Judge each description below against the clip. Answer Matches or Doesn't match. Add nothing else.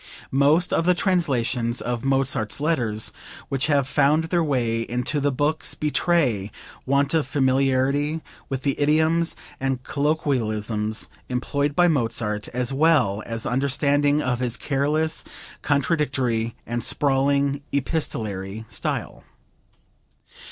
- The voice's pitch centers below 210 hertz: Matches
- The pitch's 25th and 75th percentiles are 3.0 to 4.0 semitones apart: Matches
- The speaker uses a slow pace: Matches